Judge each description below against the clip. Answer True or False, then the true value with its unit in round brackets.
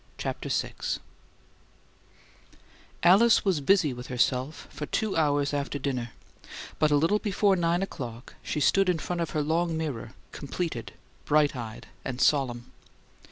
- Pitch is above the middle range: False (150 Hz)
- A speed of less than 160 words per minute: True (140 wpm)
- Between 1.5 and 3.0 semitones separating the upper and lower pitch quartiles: False (5.0 semitones)